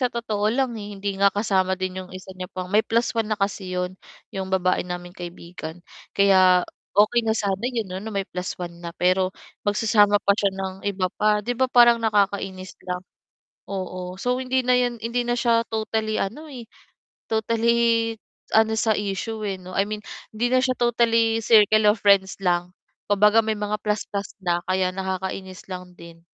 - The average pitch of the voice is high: Yes, high, 205 Hz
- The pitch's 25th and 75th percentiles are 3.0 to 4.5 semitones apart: Yes, average, 3.3 semitones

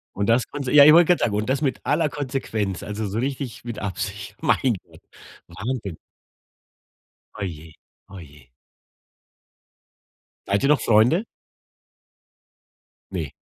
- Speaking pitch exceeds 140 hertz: No, low, 115 Hz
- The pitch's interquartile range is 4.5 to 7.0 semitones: Yes, wide, 5.6 semitones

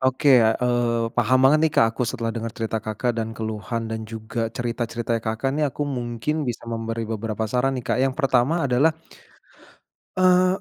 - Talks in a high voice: No, low, 120 Hz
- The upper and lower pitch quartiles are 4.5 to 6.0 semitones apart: No, average, 2.8 semitones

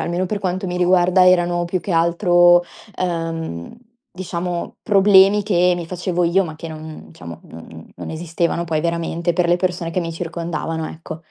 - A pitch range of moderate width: No, narrow, 1.7 semitones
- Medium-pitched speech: Yes, medium, 175 Hz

